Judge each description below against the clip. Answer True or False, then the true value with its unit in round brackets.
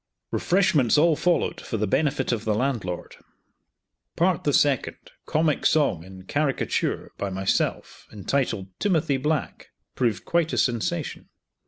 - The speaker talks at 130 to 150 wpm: True (140 wpm)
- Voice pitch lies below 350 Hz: True (135 Hz)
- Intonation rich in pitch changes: True (6.7 semitones)